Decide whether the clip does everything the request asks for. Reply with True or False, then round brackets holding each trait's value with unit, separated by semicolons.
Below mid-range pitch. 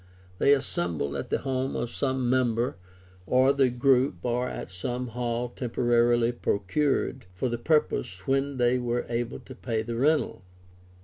True (120 Hz)